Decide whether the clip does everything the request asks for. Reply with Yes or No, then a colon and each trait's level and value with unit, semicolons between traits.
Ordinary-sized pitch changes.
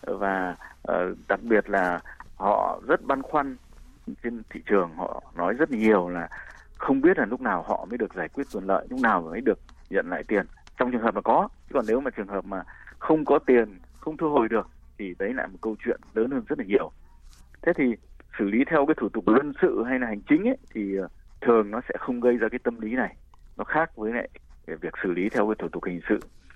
No: wide, 6.1 semitones